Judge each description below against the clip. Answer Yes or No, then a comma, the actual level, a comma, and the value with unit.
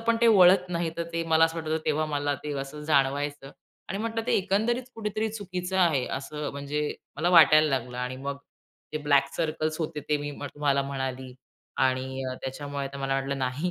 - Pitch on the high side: No, medium, 150 Hz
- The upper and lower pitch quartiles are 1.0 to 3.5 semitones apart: No, average, 3.9 semitones